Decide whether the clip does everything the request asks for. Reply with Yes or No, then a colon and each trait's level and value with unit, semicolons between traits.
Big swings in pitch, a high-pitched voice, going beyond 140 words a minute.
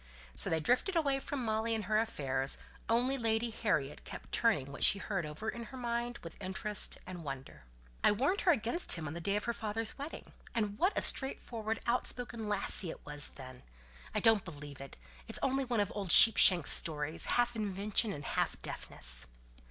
Yes: wide, 6.3 semitones; high, 215 Hz; average, 195 wpm